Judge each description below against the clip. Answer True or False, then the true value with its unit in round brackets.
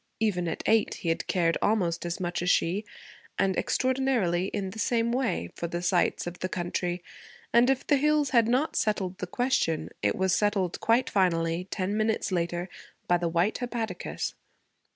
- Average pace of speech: True (175 wpm)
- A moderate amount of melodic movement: True (4.8 semitones)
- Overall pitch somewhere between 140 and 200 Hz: True (190 Hz)